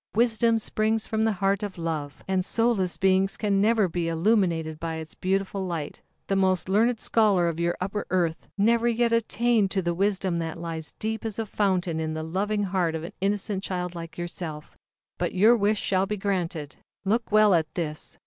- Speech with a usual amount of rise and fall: Yes, average, 3.9 semitones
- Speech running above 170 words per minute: Yes, average, 190 wpm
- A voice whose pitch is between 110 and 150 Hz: No, high, 190 Hz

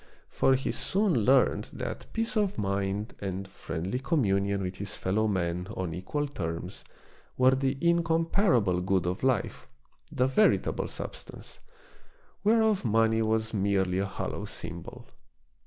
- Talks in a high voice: No, low, 110 Hz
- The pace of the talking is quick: No, average, 140 wpm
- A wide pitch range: Yes, wide, 6.3 semitones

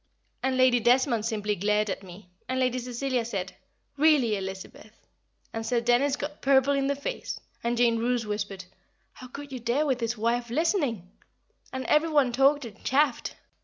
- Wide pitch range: No, average, 3.5 semitones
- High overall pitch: Yes, high, 245 Hz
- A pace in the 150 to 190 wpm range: Yes, average, 170 wpm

